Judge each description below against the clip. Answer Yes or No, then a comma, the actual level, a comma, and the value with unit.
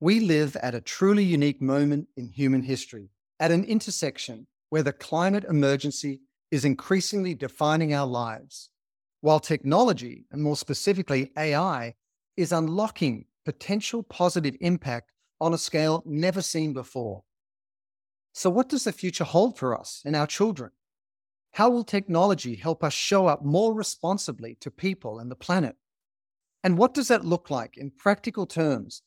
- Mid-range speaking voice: Yes, medium, 155 Hz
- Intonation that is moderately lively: No, wide, 5.8 semitones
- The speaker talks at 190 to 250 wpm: No, average, 150 wpm